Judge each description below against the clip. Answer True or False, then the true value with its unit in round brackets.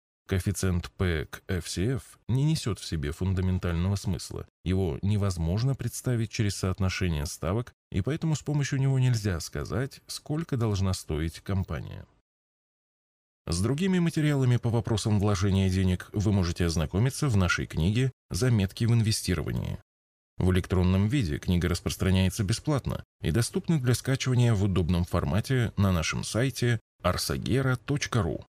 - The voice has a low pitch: True (100 Hz)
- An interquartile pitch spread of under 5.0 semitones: False (5.5 semitones)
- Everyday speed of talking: True (125 wpm)